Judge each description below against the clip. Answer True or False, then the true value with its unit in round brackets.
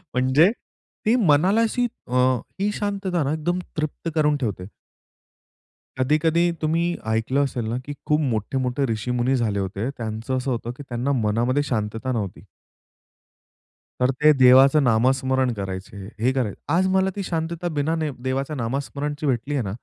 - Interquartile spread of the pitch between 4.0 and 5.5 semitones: True (4.4 semitones)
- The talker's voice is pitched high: False (135 Hz)